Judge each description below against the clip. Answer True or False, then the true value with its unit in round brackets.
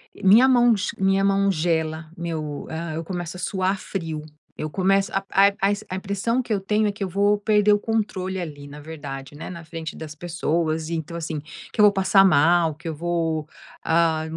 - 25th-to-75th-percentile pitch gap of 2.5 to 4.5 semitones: True (3.7 semitones)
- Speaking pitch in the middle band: True (175 Hz)